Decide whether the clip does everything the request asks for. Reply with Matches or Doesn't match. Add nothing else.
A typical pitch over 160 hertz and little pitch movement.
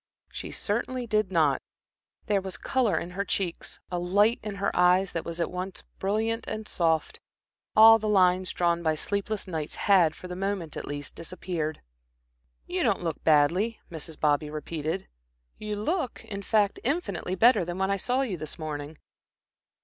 Doesn't match